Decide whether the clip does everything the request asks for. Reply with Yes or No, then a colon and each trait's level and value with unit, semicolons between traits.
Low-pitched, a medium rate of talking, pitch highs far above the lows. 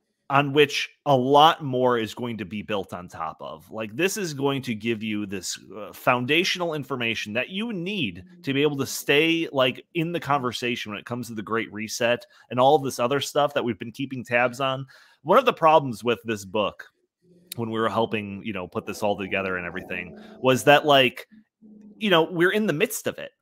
No: low, 130 Hz; fast, 220 wpm; wide, 5.9 semitones